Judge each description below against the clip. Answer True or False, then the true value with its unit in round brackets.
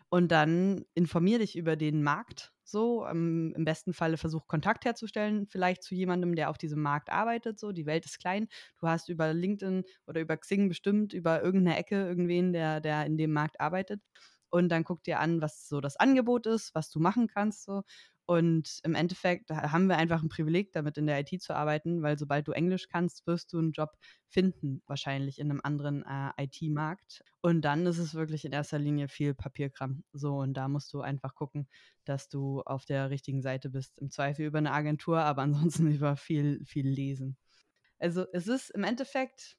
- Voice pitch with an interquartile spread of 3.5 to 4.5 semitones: True (3.8 semitones)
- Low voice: False (160 Hz)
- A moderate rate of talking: False (200 wpm)